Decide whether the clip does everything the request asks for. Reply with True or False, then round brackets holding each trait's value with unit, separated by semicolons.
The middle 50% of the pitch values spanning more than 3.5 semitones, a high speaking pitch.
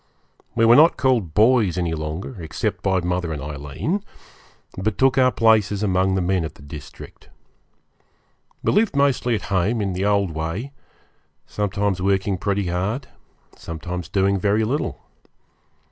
False (4.3 semitones; 95 Hz)